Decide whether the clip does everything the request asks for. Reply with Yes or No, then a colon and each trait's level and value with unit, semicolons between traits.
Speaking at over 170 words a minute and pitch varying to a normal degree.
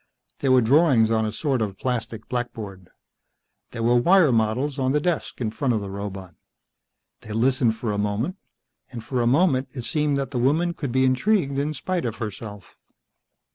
Yes: average, 185 wpm; average, 4.2 semitones